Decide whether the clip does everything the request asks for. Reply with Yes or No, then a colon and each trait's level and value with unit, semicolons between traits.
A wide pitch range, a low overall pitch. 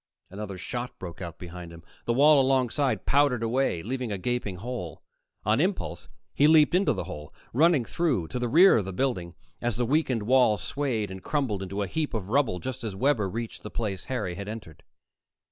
Yes: wide, 5.8 semitones; low, 115 Hz